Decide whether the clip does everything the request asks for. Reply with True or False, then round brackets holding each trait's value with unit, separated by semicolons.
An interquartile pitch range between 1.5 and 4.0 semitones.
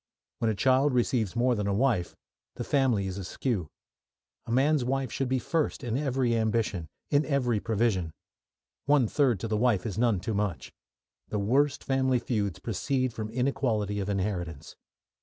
False (4.4 semitones)